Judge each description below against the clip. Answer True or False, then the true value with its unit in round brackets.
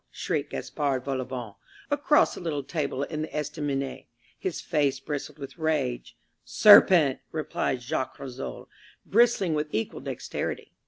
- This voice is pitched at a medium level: True (145 Hz)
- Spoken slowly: True (125 wpm)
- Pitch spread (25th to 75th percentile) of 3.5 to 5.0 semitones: False (3.1 semitones)